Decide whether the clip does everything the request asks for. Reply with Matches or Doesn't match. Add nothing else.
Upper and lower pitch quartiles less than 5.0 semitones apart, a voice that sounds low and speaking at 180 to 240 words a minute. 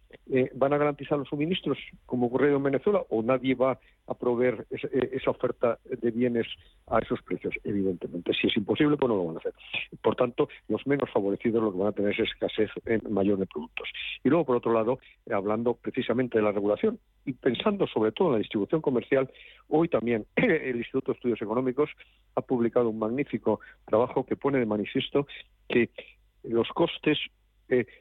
Matches